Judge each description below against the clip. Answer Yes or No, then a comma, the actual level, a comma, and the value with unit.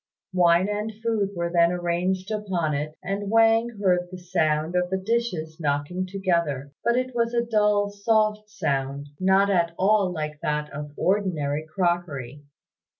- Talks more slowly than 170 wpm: Yes, average, 150 wpm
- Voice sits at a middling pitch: Yes, medium, 180 Hz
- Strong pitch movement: No, average, 4.8 semitones